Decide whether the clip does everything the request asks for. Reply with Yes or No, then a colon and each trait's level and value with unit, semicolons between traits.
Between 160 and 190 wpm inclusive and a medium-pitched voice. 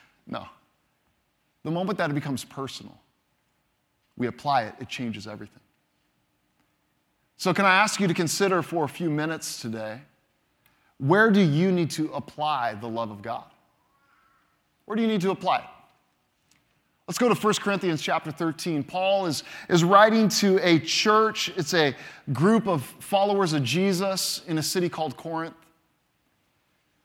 No: average, 150 wpm; medium, 165 Hz